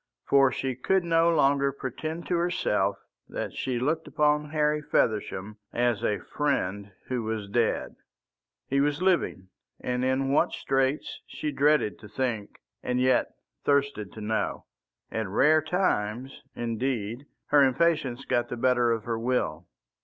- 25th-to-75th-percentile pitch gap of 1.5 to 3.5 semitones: No, average, 4.8 semitones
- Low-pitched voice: Yes, low, 130 Hz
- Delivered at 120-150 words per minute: Yes, average, 145 wpm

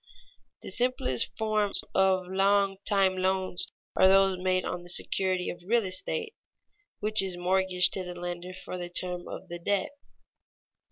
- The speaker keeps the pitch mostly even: Yes, narrow, 1.5 semitones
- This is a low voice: No, medium, 185 Hz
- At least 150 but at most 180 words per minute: Yes, average, 160 wpm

